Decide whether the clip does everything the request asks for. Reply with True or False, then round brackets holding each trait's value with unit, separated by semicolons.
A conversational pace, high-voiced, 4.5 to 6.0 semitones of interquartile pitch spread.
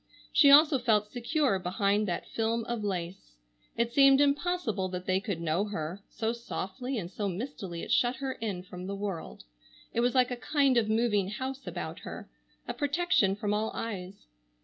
True (180 wpm; 220 Hz; 5.0 semitones)